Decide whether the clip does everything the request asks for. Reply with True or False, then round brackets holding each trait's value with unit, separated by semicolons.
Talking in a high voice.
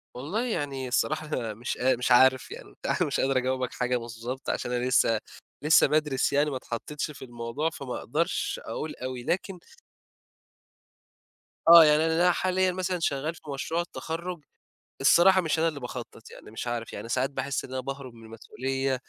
False (135 Hz)